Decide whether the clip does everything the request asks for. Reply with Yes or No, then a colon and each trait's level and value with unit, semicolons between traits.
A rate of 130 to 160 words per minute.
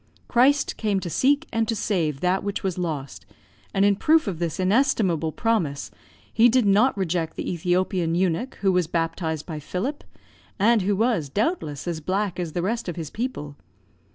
No: average, 180 wpm